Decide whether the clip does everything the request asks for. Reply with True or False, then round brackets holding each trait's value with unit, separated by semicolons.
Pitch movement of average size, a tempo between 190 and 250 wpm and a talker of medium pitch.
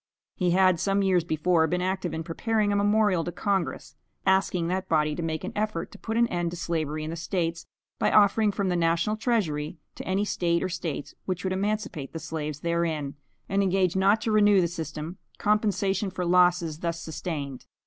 True (3.2 semitones; 195 wpm; 180 Hz)